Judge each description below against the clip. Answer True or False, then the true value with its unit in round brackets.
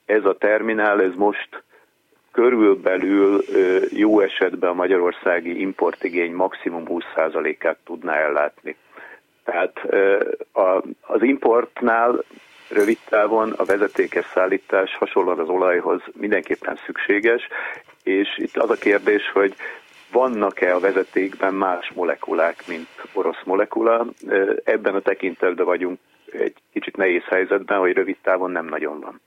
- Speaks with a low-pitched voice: False (375 Hz)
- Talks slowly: False (115 wpm)